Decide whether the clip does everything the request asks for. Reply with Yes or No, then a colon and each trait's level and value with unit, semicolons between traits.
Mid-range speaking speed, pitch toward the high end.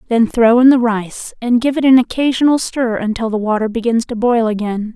No: fast, 220 wpm; high, 235 Hz